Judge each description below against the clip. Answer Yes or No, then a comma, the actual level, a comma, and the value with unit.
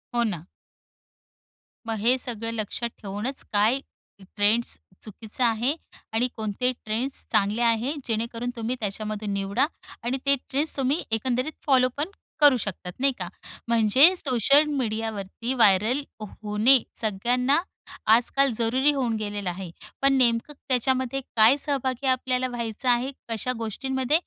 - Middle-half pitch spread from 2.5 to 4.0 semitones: Yes, average, 3.3 semitones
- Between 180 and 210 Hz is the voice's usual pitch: No, high, 235 Hz